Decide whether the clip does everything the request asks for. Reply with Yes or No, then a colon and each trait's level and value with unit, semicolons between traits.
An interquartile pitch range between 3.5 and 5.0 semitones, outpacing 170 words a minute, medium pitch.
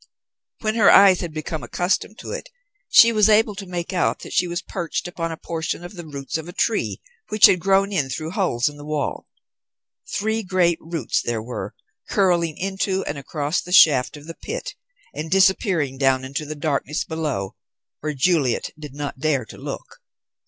Yes: average, 4.6 semitones; average, 190 wpm; medium, 165 Hz